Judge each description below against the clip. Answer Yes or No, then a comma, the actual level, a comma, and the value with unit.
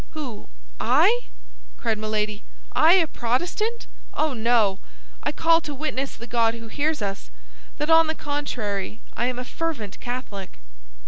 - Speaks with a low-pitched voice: No, high, 245 Hz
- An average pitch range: No, wide, 6.3 semitones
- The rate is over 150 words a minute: No, average, 140 wpm